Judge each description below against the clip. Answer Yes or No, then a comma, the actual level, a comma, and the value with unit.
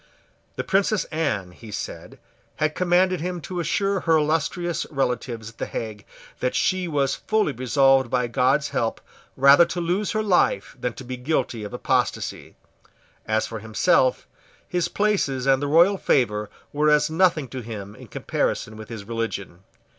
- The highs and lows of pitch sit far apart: Yes, wide, 7.0 semitones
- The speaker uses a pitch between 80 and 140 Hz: Yes, low, 135 Hz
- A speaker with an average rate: Yes, average, 160 wpm